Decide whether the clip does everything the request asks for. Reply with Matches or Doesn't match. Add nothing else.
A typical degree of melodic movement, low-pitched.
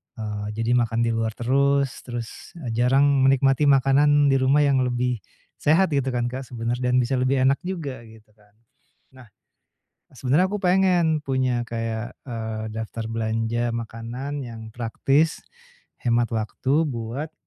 Matches